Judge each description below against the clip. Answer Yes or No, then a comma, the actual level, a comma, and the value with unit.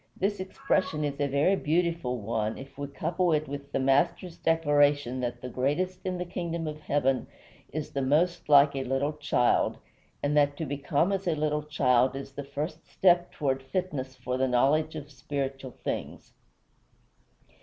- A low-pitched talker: No, medium, 145 Hz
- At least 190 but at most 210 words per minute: No, average, 170 wpm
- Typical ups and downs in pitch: Yes, average, 3.3 semitones